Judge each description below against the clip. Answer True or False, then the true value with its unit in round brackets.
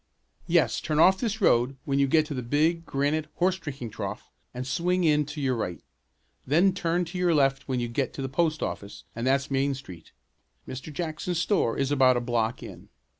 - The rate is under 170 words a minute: False (205 wpm)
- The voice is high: False (140 Hz)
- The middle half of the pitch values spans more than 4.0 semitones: True (4.4 semitones)